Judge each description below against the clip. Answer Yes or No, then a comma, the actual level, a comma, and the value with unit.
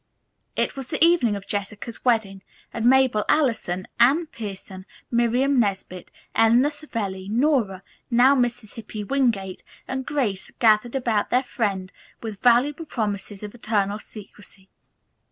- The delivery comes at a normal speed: No, slow, 130 wpm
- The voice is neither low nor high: No, high, 230 Hz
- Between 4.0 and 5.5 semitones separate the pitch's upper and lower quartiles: Yes, average, 4.3 semitones